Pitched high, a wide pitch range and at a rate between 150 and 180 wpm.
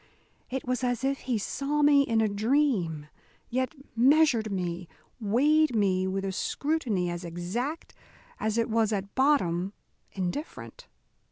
No: high, 230 Hz; wide, 6.3 semitones; average, 140 wpm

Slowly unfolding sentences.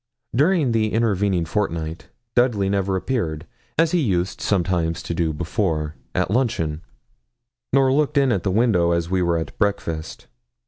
No: average, 150 wpm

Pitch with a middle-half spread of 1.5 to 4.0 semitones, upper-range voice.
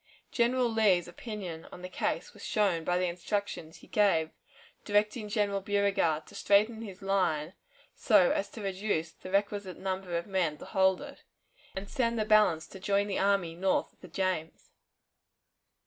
Yes: average, 2.8 semitones; high, 195 Hz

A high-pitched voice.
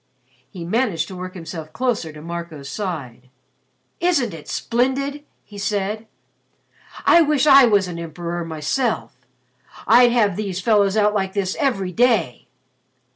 Yes: high, 200 Hz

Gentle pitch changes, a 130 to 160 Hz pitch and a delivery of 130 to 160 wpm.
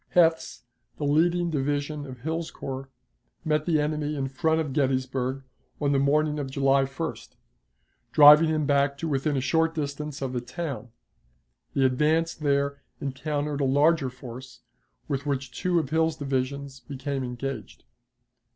Yes: narrow, 2.3 semitones; medium, 140 Hz; average, 150 wpm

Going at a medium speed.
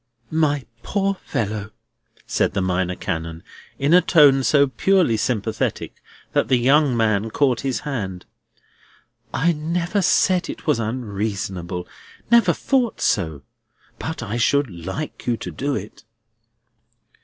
No: slow, 130 wpm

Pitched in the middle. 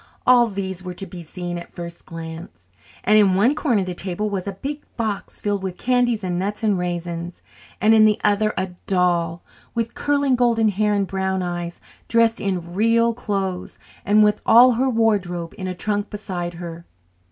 No: high, 195 Hz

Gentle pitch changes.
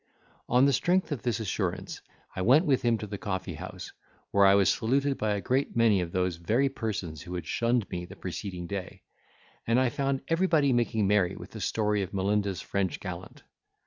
No: average, 5.0 semitones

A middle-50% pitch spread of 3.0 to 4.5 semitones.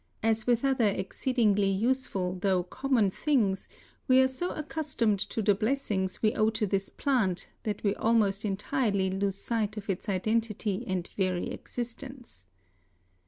Yes: average, 4.0 semitones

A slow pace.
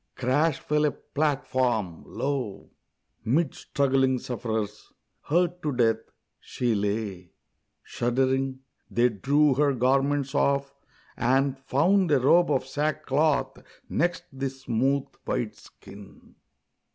Yes: slow, 105 wpm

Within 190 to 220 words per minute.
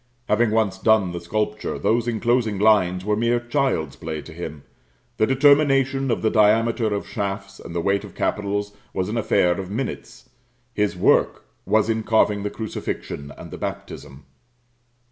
No: average, 160 wpm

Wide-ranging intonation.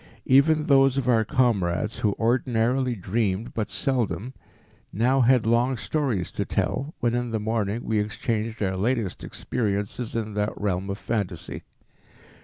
No: average, 3.4 semitones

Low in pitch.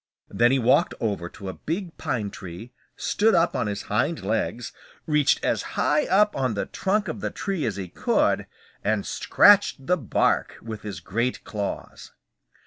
Yes: low, 120 Hz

